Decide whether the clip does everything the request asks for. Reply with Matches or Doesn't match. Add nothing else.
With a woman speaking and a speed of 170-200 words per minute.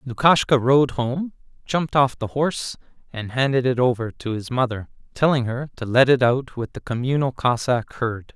Doesn't match